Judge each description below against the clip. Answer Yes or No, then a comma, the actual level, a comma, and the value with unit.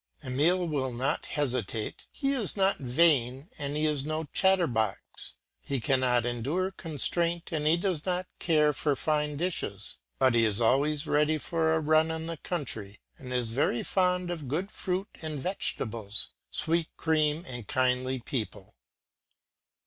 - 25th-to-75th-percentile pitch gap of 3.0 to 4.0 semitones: No, average, 4.8 semitones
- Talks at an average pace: Yes, average, 150 wpm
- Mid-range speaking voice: Yes, medium, 150 Hz